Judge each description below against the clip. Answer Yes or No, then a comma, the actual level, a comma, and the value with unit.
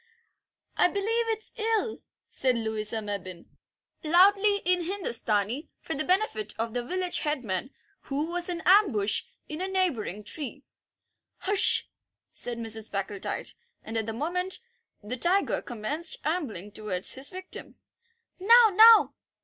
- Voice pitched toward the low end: No, very high, 300 Hz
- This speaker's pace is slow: Yes, slow, 130 wpm